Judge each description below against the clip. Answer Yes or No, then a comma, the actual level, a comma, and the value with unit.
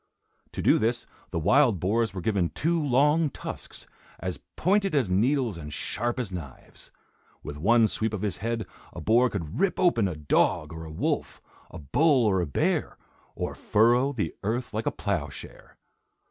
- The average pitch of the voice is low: Yes, low, 110 Hz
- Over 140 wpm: Yes, average, 175 wpm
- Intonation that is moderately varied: No, wide, 5.9 semitones